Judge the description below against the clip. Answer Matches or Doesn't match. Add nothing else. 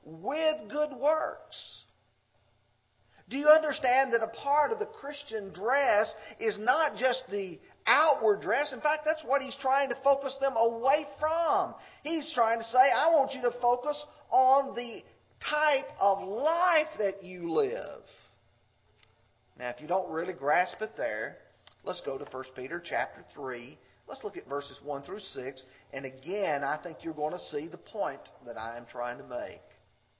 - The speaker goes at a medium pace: Matches